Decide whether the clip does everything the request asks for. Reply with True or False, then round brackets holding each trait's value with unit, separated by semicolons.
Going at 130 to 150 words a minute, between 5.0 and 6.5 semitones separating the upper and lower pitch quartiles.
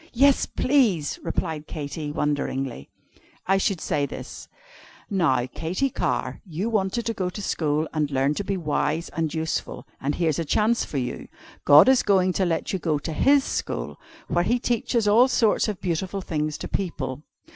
False (175 wpm; 5.6 semitones)